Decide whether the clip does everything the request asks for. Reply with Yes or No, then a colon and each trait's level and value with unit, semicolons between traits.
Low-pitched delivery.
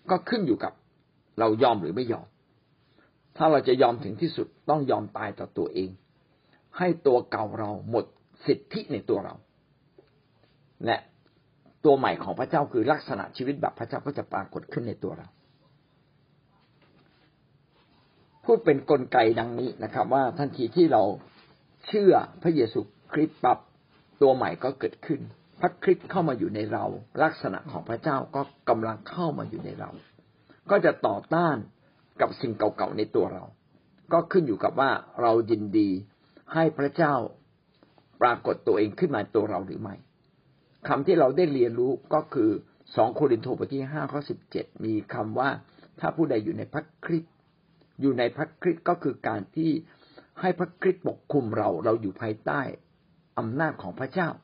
No: medium, 150 Hz